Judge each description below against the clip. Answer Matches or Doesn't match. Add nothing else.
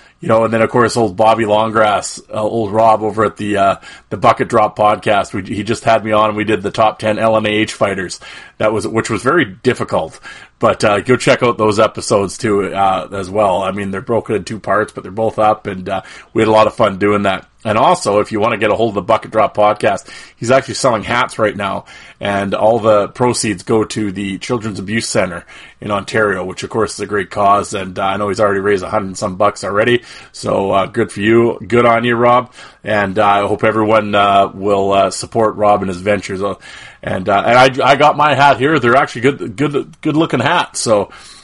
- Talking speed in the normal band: Doesn't match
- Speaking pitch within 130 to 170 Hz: Doesn't match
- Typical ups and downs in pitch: Doesn't match